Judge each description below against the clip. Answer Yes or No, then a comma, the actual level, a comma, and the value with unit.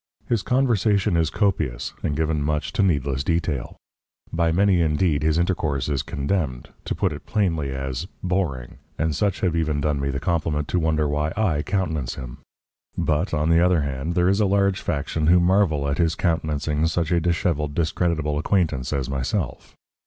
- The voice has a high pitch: No, very low, 80 Hz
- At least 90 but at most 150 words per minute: No, average, 175 wpm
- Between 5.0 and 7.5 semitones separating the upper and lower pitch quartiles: No, average, 3.6 semitones